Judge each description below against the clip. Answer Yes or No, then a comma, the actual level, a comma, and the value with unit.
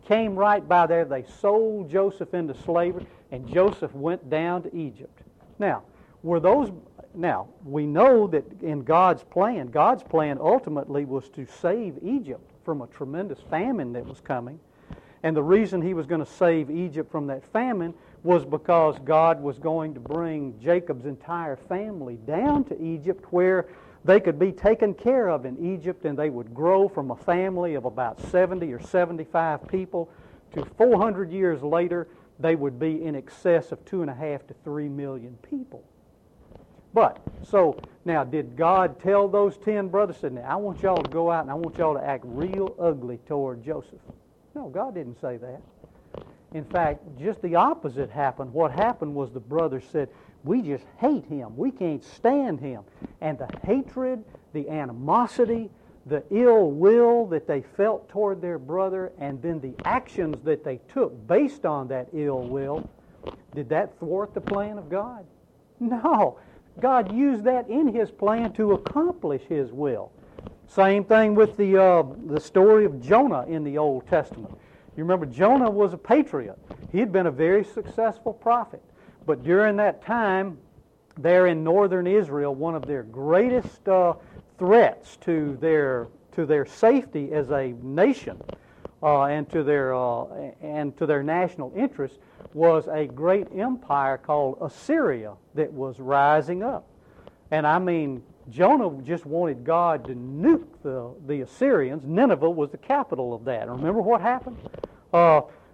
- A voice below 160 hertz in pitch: No, medium, 165 Hz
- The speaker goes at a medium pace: Yes, average, 165 wpm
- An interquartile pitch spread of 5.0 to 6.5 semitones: Yes, wide, 5.5 semitones